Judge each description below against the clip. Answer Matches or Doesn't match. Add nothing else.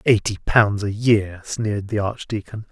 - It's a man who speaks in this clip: Matches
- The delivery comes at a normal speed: Matches